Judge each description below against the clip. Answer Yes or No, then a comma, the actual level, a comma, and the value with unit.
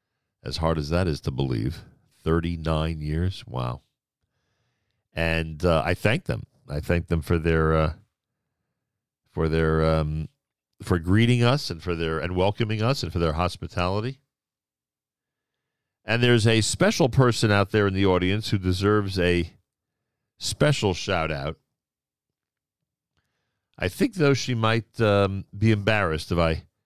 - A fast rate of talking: No, average, 140 wpm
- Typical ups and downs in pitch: No, wide, 5.7 semitones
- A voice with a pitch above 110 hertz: No, very low, 95 Hz